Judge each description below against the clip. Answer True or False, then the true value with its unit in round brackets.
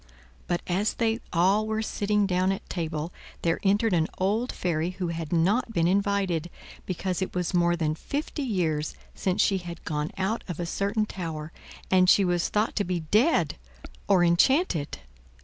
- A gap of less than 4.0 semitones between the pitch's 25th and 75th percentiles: True (3.3 semitones)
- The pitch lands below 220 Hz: True (185 Hz)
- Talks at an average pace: True (170 wpm)